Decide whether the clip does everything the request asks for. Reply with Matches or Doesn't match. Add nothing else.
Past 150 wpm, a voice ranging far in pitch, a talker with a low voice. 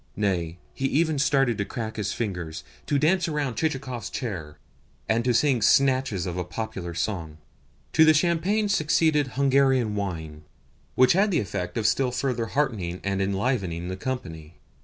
Matches